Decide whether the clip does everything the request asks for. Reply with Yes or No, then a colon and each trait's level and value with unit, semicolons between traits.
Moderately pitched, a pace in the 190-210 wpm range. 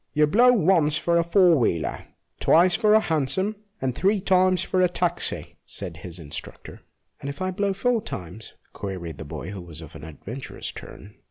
Yes: medium, 155 Hz; average, 200 wpm